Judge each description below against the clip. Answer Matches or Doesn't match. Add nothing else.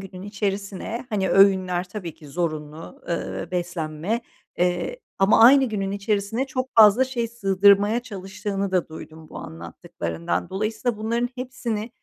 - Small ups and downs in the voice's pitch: Doesn't match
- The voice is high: Matches